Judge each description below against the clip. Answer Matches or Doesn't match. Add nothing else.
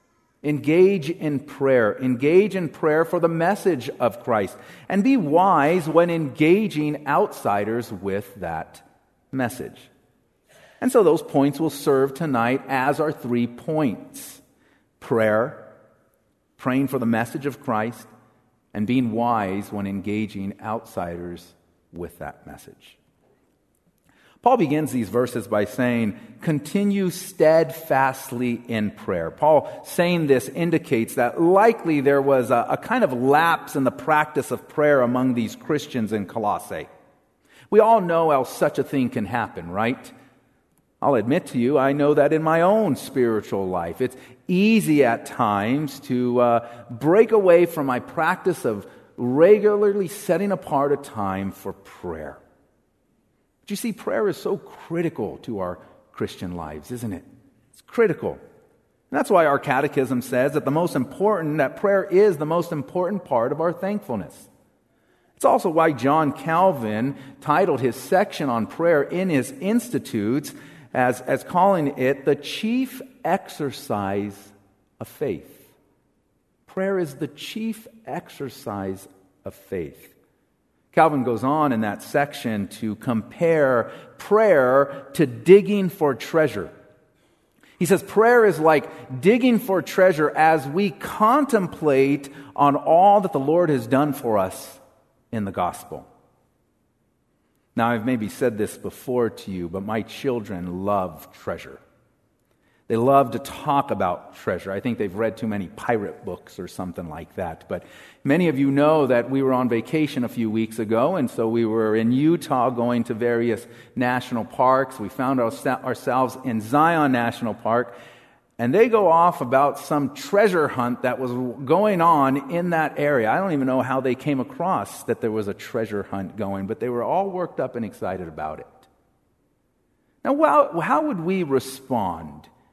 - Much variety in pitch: Matches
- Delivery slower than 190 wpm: Matches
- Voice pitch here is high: Doesn't match